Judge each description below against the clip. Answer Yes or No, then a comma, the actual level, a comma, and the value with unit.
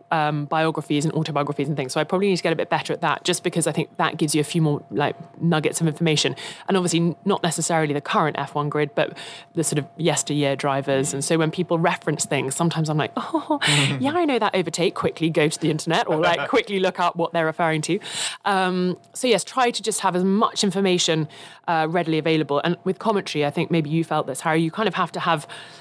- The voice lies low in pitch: No, medium, 165 Hz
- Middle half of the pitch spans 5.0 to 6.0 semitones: No, average, 3.0 semitones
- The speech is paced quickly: Yes, fast, 240 wpm